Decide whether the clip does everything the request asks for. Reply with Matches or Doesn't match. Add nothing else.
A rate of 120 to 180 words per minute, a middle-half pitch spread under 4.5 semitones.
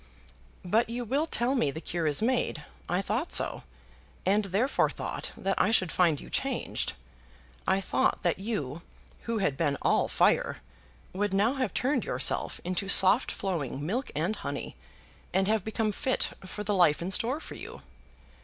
Doesn't match